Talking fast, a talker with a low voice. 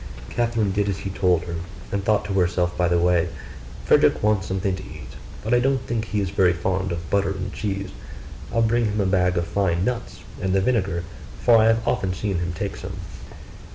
Yes: fast, 215 wpm; very low, 95 Hz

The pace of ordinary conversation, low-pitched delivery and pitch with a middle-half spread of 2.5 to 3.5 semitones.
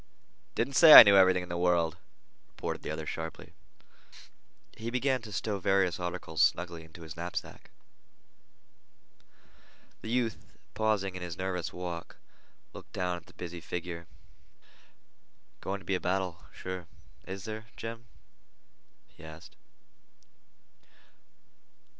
No: slow, 125 wpm; very low, 90 Hz; average, 3.0 semitones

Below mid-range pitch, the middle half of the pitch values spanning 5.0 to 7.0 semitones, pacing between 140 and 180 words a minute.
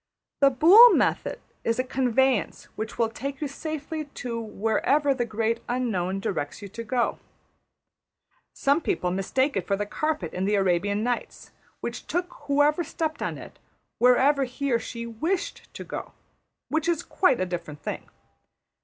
No: high, 245 Hz; wide, 5.6 semitones; average, 160 wpm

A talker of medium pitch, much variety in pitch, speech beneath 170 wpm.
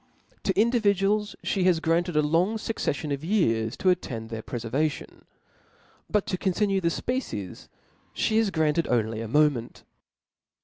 Yes: medium, 165 Hz; wide, 7.9 semitones; average, 150 wpm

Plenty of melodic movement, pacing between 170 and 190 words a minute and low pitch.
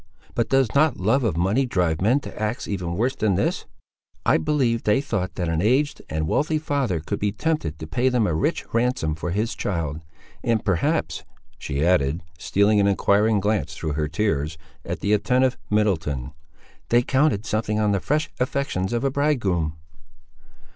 Yes: wide, 6.7 semitones; average, 175 wpm; low, 105 Hz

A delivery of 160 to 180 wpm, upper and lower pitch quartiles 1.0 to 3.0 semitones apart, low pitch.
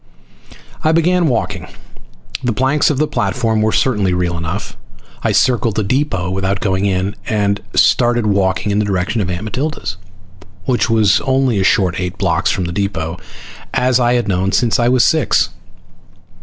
No: average, 170 wpm; average, 4.8 semitones; low, 105 Hz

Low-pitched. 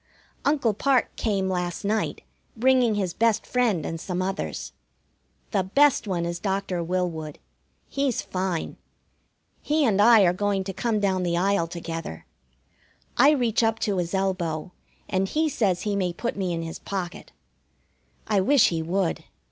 No: high, 195 Hz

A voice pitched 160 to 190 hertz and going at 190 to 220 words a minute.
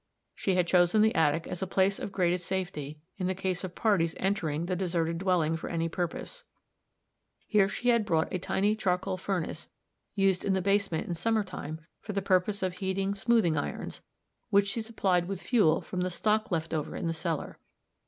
Yes: medium, 185 Hz; average, 195 wpm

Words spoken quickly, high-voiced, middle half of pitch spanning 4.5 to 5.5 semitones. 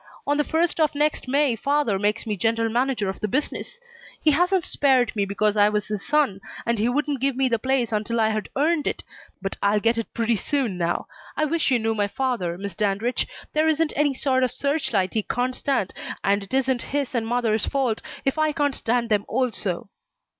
Yes: fast, 210 wpm; high, 245 Hz; average, 5.0 semitones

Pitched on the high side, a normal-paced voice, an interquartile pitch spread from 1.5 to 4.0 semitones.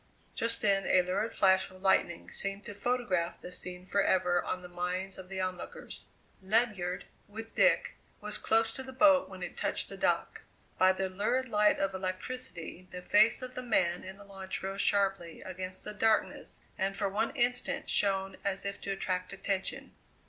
Yes: high, 195 Hz; average, 180 wpm; narrow, 2.5 semitones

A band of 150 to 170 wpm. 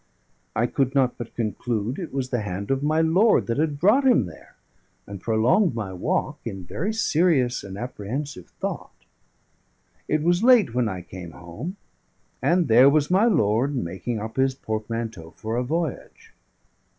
Yes: average, 160 wpm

